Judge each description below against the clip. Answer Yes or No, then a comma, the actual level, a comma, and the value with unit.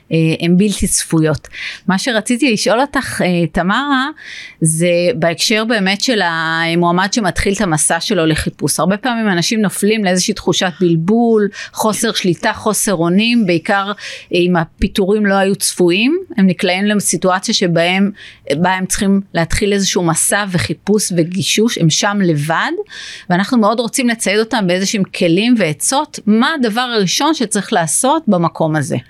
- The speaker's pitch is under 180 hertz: No, high, 195 Hz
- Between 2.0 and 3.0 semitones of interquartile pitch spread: No, average, 4.1 semitones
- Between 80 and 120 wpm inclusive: No, average, 130 wpm